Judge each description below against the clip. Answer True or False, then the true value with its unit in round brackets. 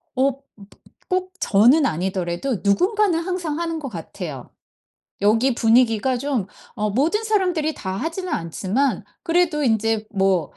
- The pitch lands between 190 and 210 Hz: False (255 Hz)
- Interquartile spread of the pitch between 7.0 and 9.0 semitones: True (8.6 semitones)